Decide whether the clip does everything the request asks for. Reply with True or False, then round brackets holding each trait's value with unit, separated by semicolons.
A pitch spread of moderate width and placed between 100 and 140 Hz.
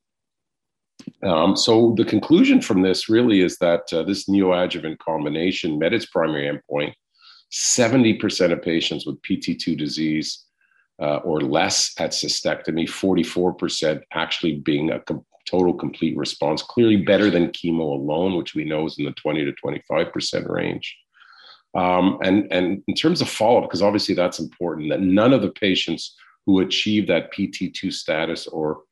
False (4.1 semitones; 90 Hz)